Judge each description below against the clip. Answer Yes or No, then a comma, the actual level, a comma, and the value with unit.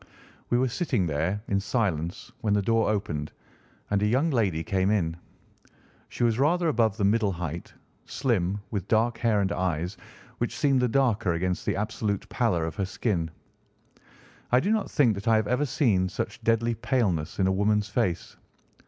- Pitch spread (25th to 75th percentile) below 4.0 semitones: No, average, 4.3 semitones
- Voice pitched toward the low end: Yes, low, 105 Hz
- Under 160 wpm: No, average, 180 wpm